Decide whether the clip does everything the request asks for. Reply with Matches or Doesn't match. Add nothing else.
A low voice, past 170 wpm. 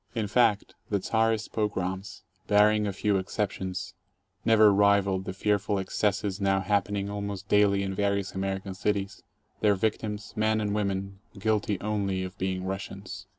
Doesn't match